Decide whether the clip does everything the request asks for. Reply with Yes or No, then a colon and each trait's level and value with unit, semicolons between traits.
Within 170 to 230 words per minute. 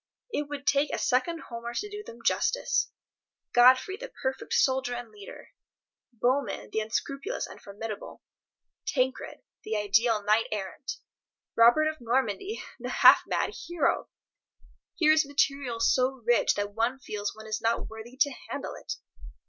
No: average, 150 wpm